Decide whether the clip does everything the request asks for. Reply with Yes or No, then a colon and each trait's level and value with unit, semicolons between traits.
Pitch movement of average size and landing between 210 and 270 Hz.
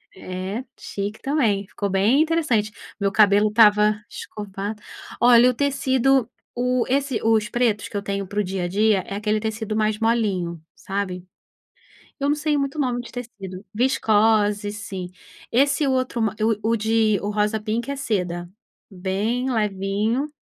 Yes: average, 3.5 semitones; high, 215 Hz